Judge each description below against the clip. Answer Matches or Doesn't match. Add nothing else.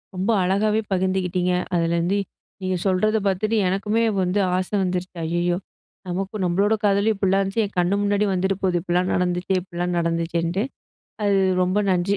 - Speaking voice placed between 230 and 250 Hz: Doesn't match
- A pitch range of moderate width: Doesn't match